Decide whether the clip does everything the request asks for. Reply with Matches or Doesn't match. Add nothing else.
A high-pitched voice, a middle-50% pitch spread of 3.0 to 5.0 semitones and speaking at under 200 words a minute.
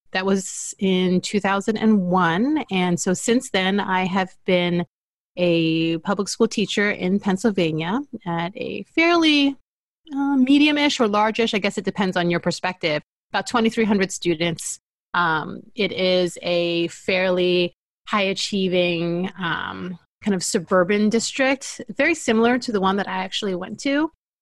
Matches